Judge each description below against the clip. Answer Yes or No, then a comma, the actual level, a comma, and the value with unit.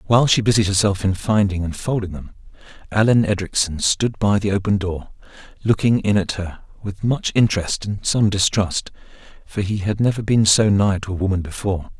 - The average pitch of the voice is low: Yes, low, 100 Hz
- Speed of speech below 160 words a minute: No, average, 185 wpm